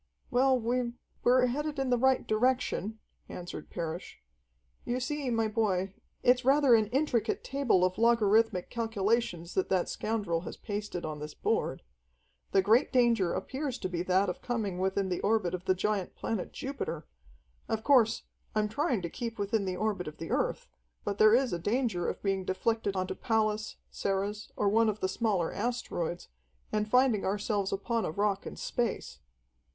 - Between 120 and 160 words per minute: No, average, 170 wpm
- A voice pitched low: No, high, 215 Hz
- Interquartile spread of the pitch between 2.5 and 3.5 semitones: No, average, 4.1 semitones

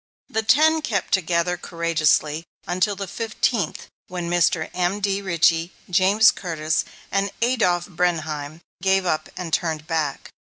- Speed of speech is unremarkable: No, slow, 125 wpm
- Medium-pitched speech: Yes, medium, 175 Hz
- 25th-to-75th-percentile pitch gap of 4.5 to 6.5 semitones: No, average, 3.3 semitones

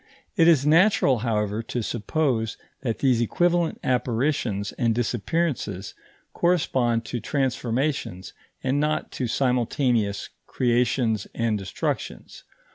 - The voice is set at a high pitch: No, low, 125 Hz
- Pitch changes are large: No, average, 4.1 semitones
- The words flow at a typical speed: No, slow, 105 wpm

